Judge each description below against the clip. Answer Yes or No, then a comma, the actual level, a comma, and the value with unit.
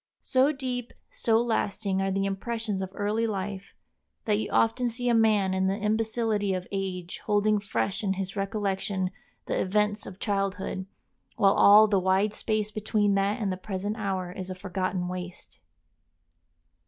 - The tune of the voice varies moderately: No, narrow, 2.2 semitones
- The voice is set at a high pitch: Yes, high, 200 Hz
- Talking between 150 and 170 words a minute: Yes, average, 160 wpm